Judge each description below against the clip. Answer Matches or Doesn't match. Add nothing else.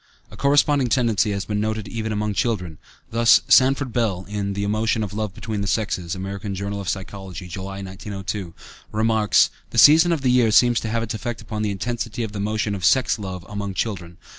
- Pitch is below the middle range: Matches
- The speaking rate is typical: Matches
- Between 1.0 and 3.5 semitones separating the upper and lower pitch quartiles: Matches